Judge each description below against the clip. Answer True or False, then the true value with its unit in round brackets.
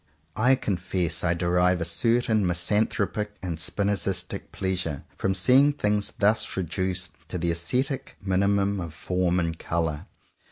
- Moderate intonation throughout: True (3.1 semitones)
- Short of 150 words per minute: True (135 wpm)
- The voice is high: False (95 Hz)